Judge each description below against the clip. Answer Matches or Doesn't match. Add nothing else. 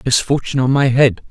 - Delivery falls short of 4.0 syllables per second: Doesn't match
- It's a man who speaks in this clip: Matches